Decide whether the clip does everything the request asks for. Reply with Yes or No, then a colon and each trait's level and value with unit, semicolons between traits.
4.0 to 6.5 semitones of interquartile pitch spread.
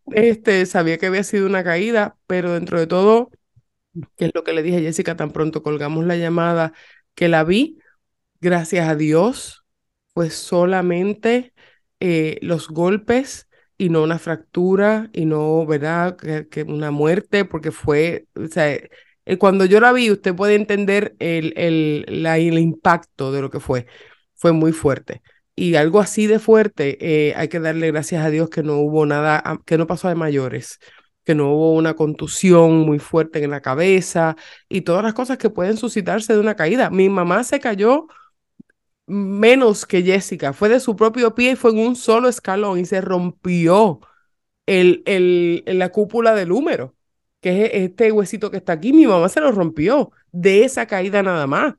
Yes: average, 4.7 semitones